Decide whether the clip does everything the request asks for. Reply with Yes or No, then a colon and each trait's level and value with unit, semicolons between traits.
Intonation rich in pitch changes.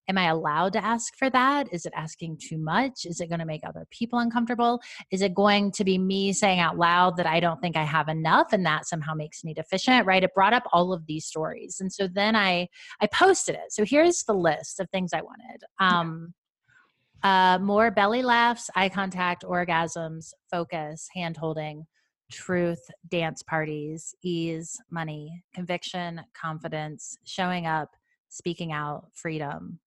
No: average, 3.7 semitones